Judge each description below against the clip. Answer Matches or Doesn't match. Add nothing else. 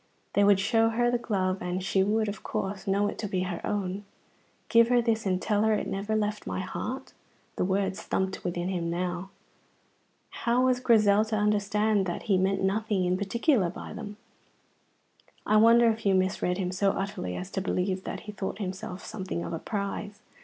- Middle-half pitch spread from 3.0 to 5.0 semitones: Doesn't match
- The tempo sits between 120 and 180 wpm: Doesn't match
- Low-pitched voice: Doesn't match